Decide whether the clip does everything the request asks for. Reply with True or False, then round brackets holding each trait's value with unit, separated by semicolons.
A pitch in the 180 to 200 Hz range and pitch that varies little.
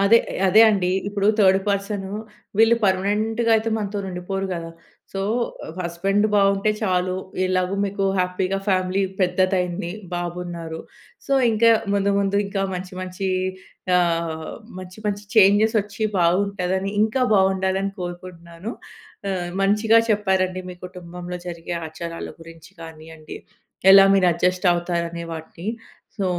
True (185 Hz; 2.2 semitones)